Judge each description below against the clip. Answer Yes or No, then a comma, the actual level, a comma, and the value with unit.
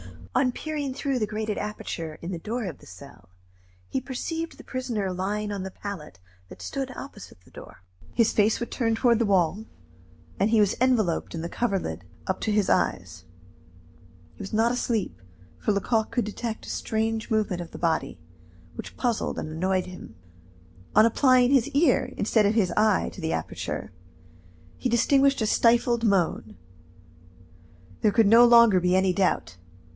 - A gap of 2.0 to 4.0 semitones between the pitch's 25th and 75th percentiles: No, average, 4.4 semitones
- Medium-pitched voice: No, high, 215 Hz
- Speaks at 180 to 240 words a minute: No, average, 170 wpm